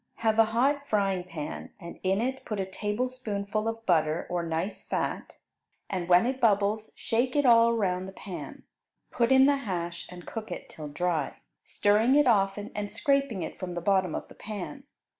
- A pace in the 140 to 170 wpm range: No, average, 185 wpm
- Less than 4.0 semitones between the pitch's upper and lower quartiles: No, average, 4.4 semitones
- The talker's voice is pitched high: Yes, high, 205 Hz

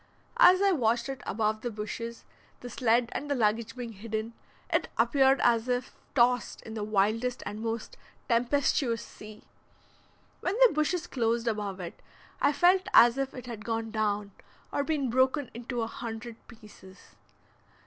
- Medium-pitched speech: No, high, 235 Hz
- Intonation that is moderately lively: Yes, average, 3.0 semitones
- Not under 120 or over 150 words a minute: No, average, 160 wpm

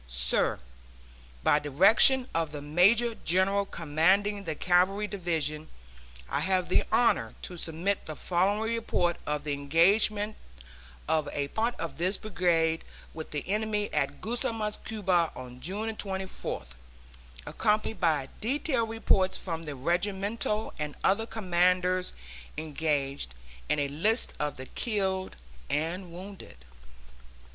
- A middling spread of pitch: Yes, average, 5.0 semitones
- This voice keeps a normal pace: No, slow, 125 wpm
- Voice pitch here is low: No, medium, 180 Hz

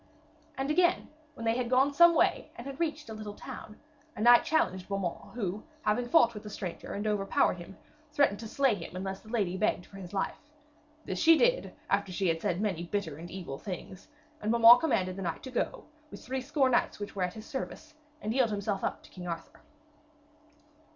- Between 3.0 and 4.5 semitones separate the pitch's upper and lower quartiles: No, wide, 5.4 semitones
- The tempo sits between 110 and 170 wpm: No, fast, 205 wpm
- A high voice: Yes, high, 215 Hz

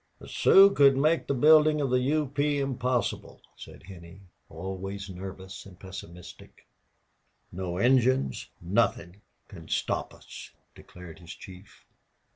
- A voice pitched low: Yes, low, 100 Hz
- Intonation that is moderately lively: No, wide, 6.9 semitones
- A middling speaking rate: No, slow, 125 wpm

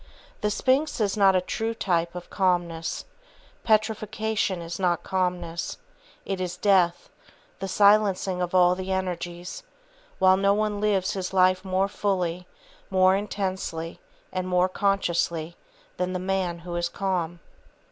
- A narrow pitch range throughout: Yes, narrow, 2.0 semitones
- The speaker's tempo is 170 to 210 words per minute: No, slow, 135 wpm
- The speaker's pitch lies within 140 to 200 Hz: Yes, medium, 185 Hz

